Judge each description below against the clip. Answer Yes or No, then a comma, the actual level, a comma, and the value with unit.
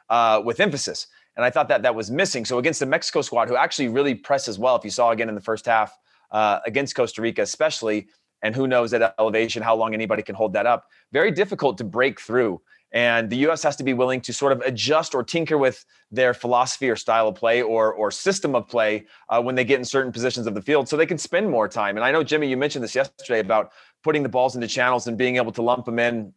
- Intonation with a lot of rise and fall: No, average, 3.1 semitones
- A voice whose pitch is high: No, low, 125 Hz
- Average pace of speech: No, fast, 255 wpm